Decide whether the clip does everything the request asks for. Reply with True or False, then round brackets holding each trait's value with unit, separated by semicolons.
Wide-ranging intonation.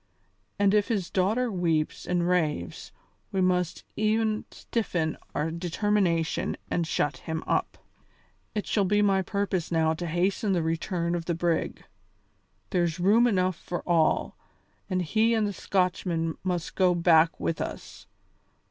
False (3.3 semitones)